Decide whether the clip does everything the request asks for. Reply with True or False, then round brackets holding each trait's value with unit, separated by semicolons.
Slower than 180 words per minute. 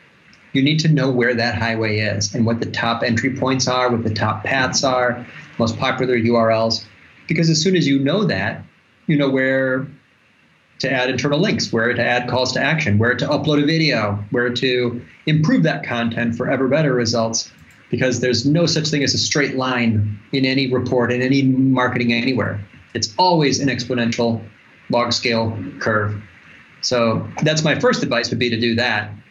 False (185 wpm)